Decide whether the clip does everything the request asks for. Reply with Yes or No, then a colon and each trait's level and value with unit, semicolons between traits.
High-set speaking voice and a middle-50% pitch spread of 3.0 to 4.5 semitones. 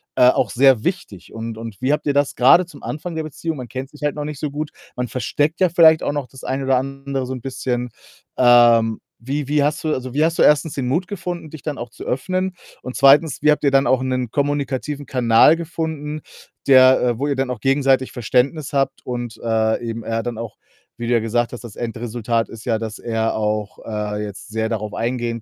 No: low, 130 Hz; average, 3.9 semitones